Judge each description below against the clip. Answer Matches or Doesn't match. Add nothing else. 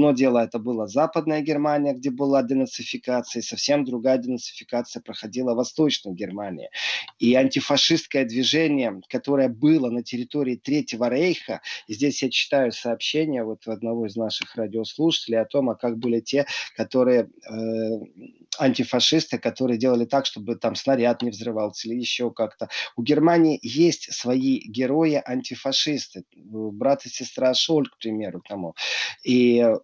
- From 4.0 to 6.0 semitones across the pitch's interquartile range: Doesn't match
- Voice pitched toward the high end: Doesn't match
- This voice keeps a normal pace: Matches